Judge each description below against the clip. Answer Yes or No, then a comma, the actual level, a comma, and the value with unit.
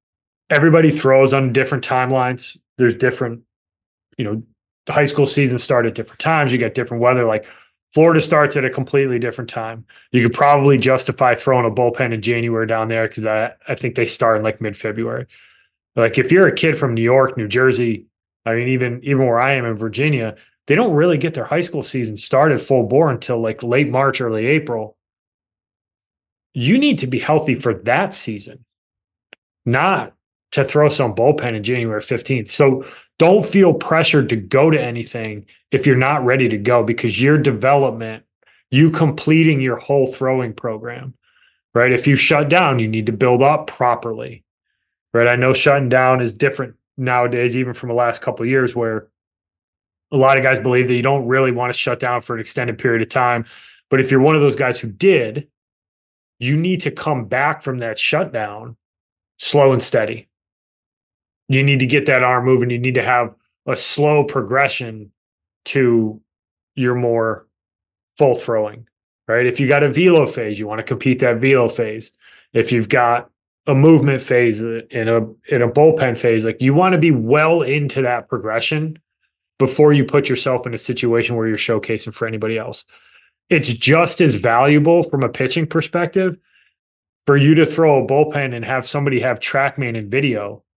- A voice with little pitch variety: No, average, 3.6 semitones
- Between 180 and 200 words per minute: Yes, average, 185 wpm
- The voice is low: Yes, low, 125 Hz